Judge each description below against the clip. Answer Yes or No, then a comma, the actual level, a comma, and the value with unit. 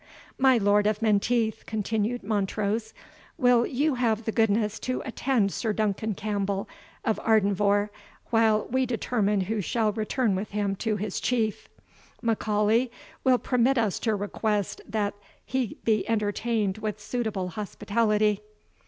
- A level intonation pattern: Yes, narrow, 2.1 semitones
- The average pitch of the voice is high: Yes, high, 215 Hz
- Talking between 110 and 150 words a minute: Yes, slow, 135 wpm